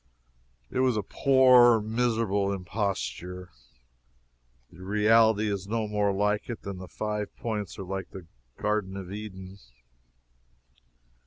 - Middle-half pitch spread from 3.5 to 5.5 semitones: No, narrow, 2.5 semitones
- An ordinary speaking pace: No, slow, 120 wpm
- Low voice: Yes, low, 105 Hz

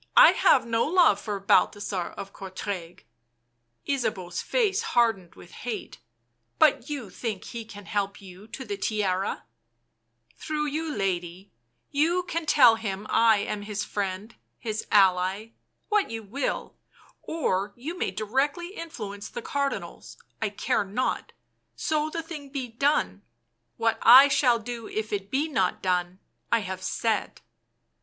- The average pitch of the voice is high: Yes, high, 215 Hz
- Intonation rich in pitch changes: Yes, wide, 6.4 semitones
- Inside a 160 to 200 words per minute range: No, average, 150 wpm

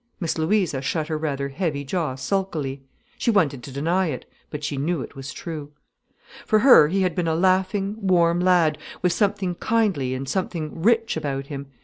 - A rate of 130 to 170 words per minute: No, average, 185 wpm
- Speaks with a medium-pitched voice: Yes, medium, 165 Hz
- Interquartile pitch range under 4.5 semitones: No, average, 4.9 semitones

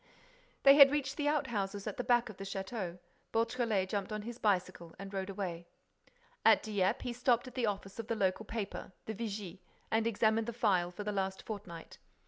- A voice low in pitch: No, high, 210 Hz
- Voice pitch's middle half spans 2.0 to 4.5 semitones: Yes, average, 3.4 semitones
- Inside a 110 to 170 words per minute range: No, average, 200 wpm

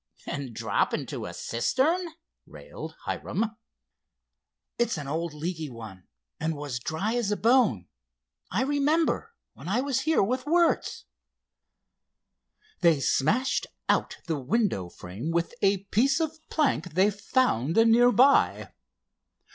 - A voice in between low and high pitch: No, high, 200 Hz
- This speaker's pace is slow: Yes, slow, 125 wpm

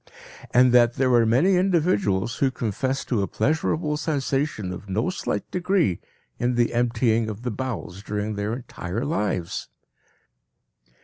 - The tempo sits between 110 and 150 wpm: Yes, average, 140 wpm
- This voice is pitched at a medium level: No, low, 120 Hz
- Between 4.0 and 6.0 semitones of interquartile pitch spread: Yes, average, 4.7 semitones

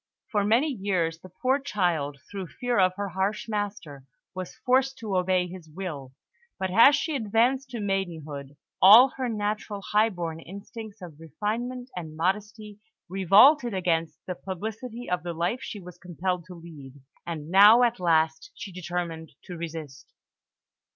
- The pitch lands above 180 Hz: Yes, high, 190 Hz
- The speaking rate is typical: Yes, average, 155 wpm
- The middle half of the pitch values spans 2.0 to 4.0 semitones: No, average, 4.5 semitones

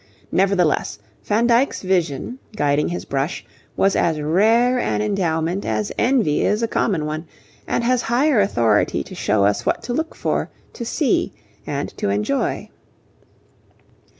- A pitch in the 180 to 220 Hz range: Yes, high, 190 Hz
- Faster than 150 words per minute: No, average, 145 wpm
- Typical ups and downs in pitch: No, wide, 7.7 semitones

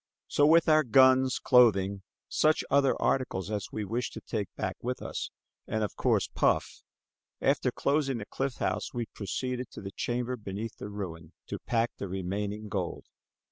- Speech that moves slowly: No, average, 170 wpm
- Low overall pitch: Yes, low, 115 Hz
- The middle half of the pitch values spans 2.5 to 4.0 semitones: No, average, 4.5 semitones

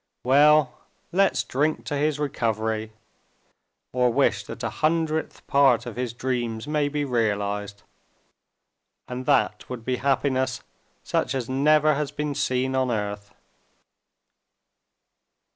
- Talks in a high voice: No, low, 130 Hz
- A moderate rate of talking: No, slow, 115 wpm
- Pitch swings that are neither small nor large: Yes, average, 3.9 semitones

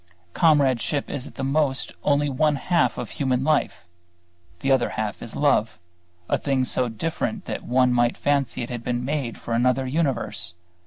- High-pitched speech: No, low, 130 Hz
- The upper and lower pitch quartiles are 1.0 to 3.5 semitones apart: Yes, average, 3.1 semitones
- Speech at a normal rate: Yes, average, 170 wpm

